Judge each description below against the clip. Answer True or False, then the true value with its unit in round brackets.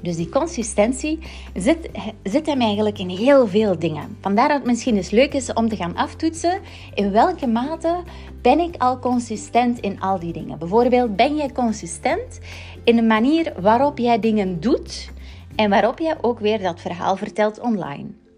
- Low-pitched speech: False (225 Hz)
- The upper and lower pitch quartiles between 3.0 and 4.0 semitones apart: False (4.8 semitones)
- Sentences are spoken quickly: False (175 wpm)